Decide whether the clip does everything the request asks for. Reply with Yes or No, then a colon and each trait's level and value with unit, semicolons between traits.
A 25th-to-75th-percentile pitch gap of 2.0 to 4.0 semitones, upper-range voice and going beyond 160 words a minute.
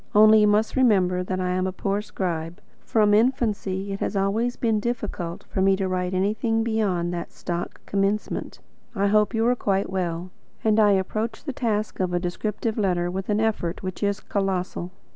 Yes: average, 2.8 semitones; high, 200 Hz; average, 185 wpm